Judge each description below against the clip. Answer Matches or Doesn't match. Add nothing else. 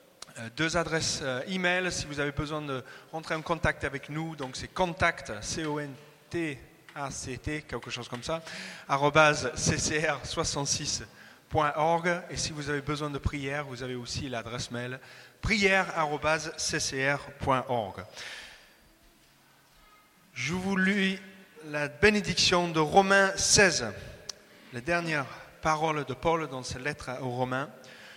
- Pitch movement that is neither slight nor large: Matches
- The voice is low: Doesn't match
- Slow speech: Matches